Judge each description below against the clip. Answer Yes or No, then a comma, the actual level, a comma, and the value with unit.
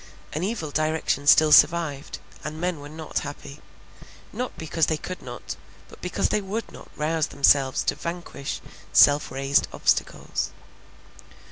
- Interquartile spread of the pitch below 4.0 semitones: Yes, average, 2.8 semitones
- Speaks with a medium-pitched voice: Yes, medium, 155 Hz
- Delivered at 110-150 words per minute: Yes, average, 140 wpm